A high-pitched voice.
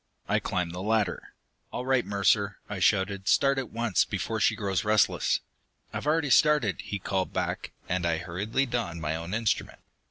No: low, 100 Hz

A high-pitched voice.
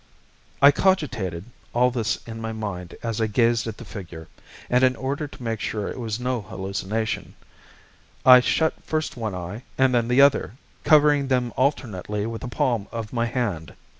No: low, 115 Hz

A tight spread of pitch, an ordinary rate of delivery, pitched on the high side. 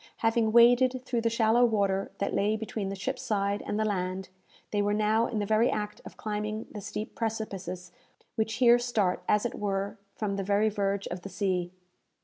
Yes: narrow, 2.2 semitones; average, 195 wpm; high, 210 Hz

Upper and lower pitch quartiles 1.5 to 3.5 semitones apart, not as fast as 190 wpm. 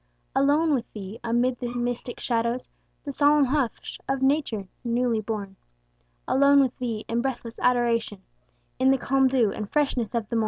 Yes: average, 2.8 semitones; average, 165 wpm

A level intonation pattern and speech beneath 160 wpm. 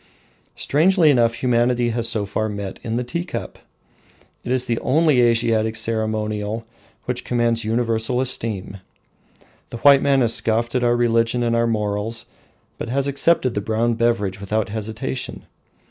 Yes: narrow, 2.1 semitones; average, 150 wpm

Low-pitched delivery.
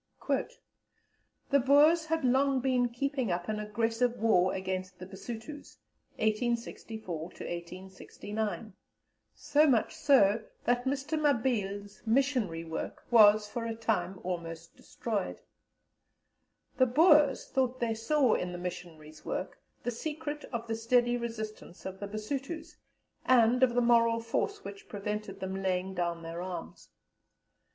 No: high, 225 Hz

